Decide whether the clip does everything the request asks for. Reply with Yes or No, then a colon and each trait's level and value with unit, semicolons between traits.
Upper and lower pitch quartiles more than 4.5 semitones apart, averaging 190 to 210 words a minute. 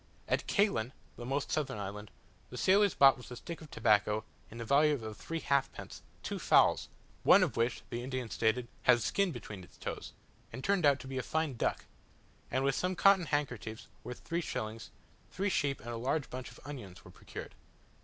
Yes: average, 4.9 semitones; average, 195 wpm